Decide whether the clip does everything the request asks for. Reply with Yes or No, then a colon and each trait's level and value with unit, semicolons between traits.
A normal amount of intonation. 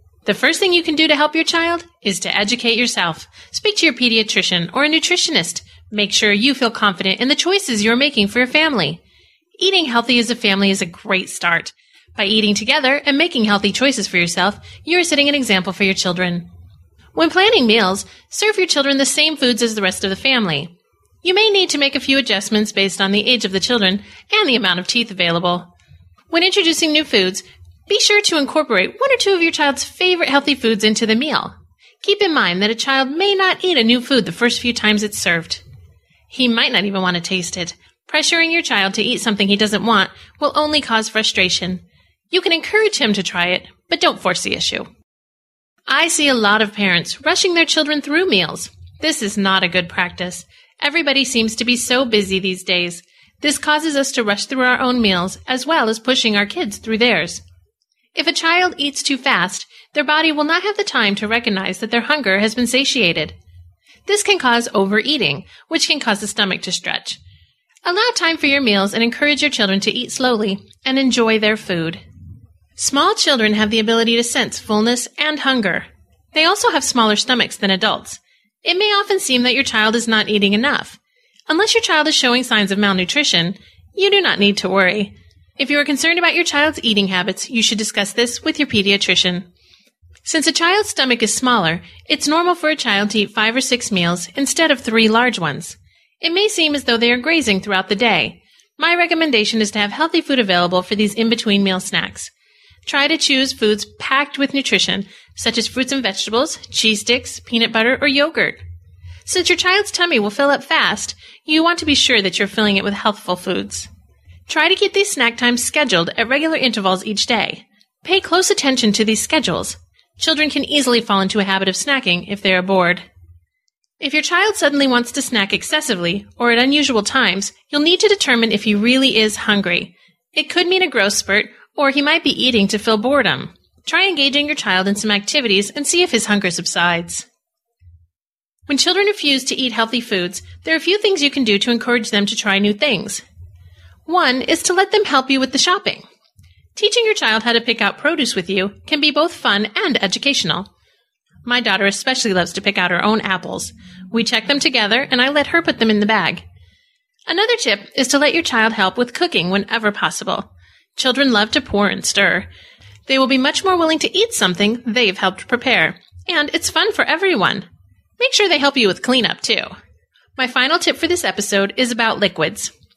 No: wide, 7.1 semitones